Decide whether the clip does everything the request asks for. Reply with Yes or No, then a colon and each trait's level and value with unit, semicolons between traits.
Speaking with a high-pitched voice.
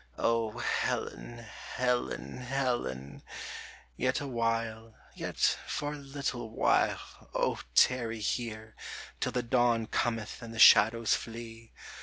No: low, 115 Hz